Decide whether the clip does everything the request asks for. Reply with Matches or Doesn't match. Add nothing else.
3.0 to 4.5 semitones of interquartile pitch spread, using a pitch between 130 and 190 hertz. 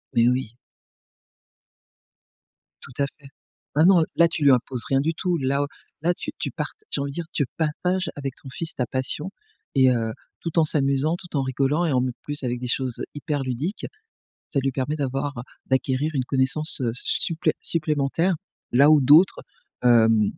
Matches